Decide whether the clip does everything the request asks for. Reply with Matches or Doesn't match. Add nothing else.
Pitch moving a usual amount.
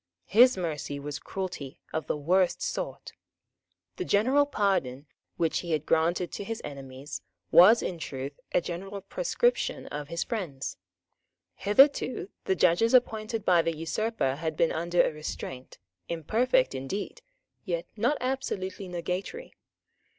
Doesn't match